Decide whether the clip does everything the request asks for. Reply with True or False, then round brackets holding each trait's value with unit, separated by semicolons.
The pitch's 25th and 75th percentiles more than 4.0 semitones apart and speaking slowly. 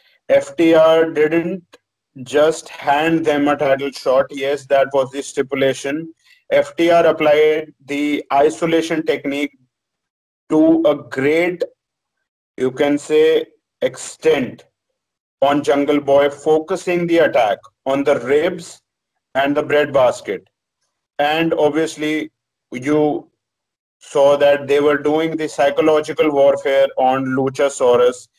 False (2.7 semitones; 105 wpm)